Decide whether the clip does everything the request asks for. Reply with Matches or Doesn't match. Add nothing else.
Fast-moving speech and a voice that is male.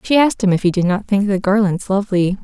Doesn't match